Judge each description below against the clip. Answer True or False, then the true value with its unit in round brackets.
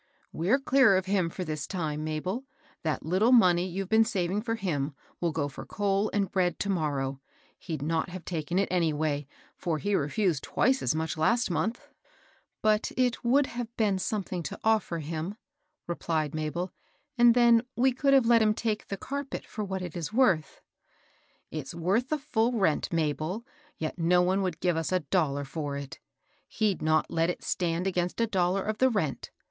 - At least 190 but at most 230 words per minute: True (195 wpm)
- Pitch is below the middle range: False (185 Hz)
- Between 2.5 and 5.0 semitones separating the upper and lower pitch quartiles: False (5.5 semitones)